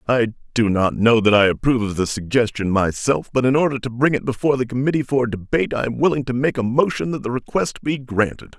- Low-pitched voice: Yes, low, 120 Hz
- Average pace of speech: No, fast, 240 wpm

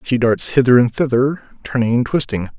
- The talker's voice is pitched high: No, low, 125 Hz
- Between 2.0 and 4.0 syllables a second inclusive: No, 5.4 syllables/s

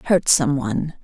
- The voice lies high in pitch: No, medium, 145 Hz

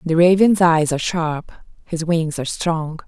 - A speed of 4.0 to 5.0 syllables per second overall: Yes, 4.6 syllables/s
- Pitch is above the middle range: No, medium, 165 Hz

